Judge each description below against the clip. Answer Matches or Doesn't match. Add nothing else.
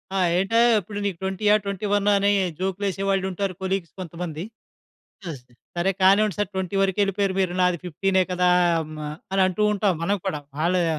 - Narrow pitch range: Matches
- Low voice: Doesn't match